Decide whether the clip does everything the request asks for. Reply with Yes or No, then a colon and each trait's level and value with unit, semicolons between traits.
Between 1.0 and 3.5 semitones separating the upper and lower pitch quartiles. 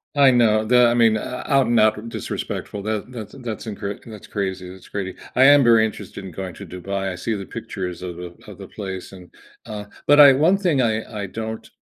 No: average, 3.9 semitones